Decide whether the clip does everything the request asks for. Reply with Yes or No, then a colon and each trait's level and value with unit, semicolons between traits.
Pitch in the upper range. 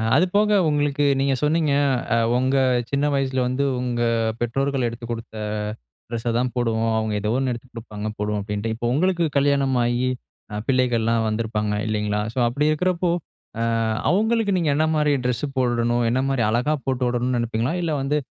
No: low, 125 Hz